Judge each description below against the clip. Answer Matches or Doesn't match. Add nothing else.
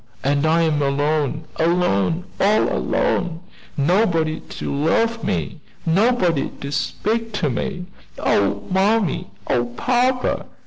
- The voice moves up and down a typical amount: Doesn't match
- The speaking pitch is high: Doesn't match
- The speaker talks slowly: Matches